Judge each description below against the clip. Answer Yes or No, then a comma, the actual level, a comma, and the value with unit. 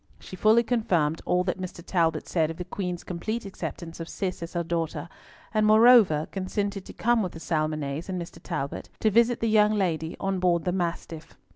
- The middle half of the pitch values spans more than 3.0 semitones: Yes, average, 4.1 semitones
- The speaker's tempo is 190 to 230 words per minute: Yes, average, 195 wpm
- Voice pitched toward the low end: No, medium, 180 Hz